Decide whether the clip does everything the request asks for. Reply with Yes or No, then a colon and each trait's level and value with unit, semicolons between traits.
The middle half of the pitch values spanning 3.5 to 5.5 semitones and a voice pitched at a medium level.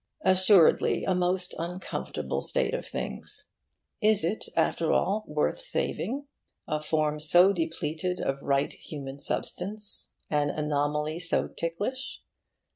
Yes: average, 4.2 semitones; medium, 170 Hz